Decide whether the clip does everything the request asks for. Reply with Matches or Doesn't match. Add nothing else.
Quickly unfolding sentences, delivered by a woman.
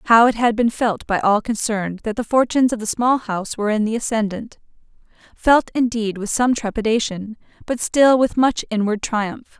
Doesn't match